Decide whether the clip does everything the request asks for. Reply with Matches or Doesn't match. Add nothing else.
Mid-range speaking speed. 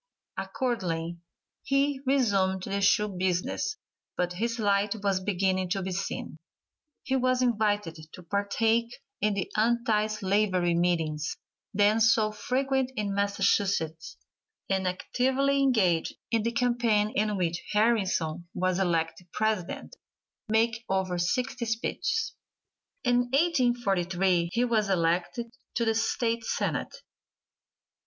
Doesn't match